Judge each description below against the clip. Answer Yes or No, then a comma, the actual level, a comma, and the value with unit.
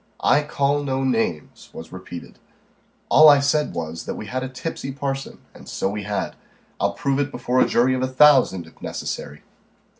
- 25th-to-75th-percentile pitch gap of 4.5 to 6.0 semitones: Yes, average, 5.2 semitones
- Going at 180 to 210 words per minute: Yes, average, 185 wpm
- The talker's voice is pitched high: No, low, 130 Hz